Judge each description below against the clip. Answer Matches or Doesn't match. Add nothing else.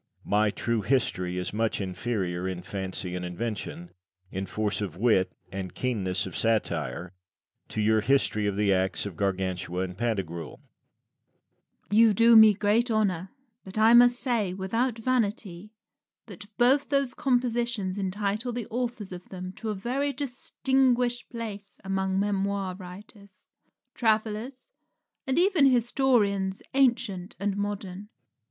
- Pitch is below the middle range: Doesn't match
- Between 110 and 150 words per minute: Matches